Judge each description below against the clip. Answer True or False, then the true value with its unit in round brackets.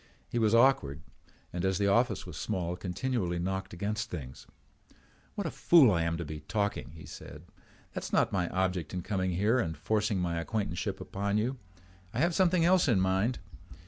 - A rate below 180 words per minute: False (185 wpm)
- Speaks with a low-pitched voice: True (95 Hz)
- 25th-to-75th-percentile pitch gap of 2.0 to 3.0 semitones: False (4.8 semitones)